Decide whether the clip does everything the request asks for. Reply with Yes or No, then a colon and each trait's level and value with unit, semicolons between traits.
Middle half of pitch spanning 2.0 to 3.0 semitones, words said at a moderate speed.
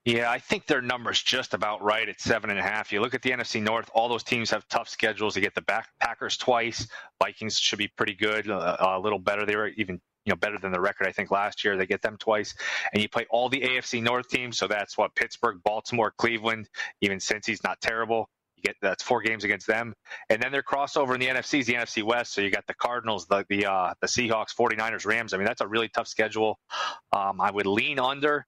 No: narrow, 2.5 semitones; fast, 250 wpm